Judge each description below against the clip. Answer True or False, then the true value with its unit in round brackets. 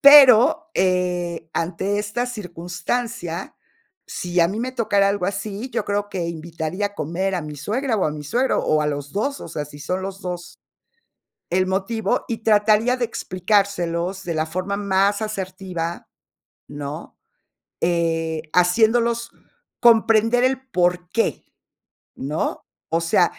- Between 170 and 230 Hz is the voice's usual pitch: True (190 Hz)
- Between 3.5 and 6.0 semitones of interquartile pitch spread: True (4.5 semitones)